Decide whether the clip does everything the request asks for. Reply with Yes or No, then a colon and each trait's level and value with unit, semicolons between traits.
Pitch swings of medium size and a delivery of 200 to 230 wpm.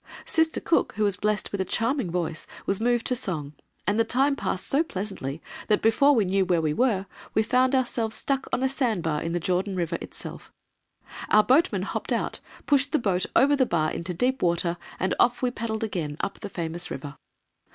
No: wide, 6.4 semitones; fast, 205 wpm